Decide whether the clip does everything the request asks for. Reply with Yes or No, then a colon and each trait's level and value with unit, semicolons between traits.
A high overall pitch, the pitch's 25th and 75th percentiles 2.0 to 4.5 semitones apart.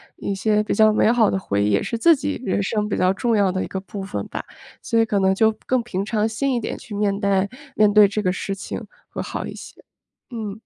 Yes: high, 210 Hz; narrow, 2.4 semitones